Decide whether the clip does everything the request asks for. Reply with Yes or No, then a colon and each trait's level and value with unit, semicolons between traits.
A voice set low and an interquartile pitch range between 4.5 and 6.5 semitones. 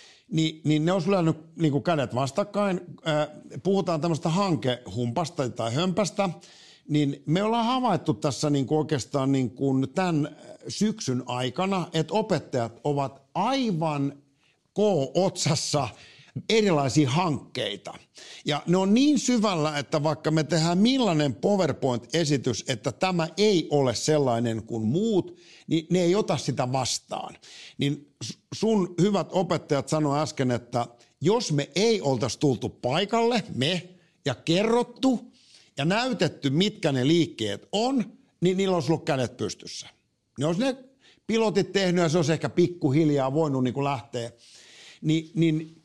No: medium, 160 Hz; average, 5.2 semitones